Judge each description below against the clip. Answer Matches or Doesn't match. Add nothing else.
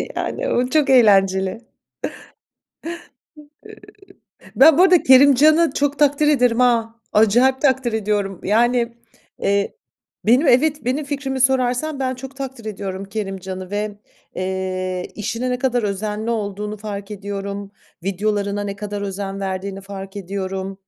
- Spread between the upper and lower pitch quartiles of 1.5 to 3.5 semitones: Doesn't match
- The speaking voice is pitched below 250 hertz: Matches